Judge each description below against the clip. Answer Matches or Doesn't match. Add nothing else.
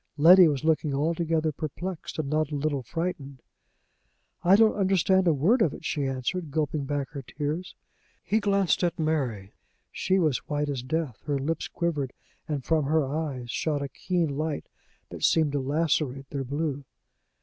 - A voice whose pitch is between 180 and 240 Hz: Doesn't match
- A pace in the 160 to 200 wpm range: Matches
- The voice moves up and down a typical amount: Matches